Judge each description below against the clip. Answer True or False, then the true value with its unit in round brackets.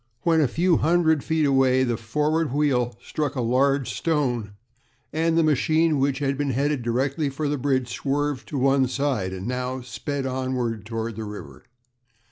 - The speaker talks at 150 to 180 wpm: True (170 wpm)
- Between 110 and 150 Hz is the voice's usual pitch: True (135 Hz)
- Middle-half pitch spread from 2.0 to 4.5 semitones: True (3.2 semitones)